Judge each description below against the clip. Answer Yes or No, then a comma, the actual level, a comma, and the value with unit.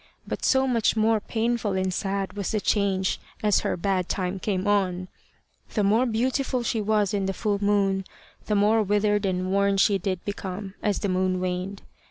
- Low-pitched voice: No, high, 200 Hz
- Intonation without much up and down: Yes, narrow, 2.0 semitones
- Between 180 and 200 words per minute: Yes, average, 185 wpm